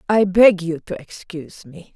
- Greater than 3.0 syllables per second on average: Yes, 4.5 syllables/s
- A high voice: No, medium, 180 Hz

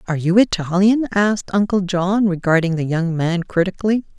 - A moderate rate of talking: Yes, average, 160 wpm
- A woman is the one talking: Yes, female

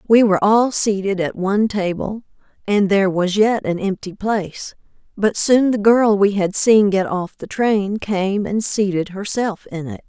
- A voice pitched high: Yes, high, 205 Hz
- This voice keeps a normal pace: Yes, average, 185 wpm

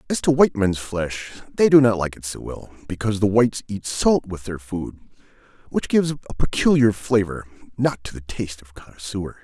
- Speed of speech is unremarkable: Yes, average, 195 wpm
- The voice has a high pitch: No, low, 105 Hz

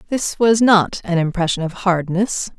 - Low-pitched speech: No, high, 190 Hz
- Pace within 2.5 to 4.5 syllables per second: Yes, 4.4 syllables/s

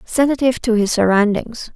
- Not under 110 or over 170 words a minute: Yes, slow, 135 wpm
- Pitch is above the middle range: Yes, high, 230 Hz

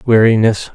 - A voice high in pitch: No, low, 110 Hz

